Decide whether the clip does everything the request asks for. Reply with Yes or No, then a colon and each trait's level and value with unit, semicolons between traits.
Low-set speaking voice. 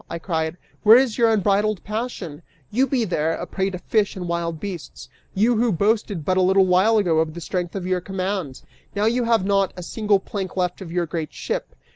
No: high, 190 Hz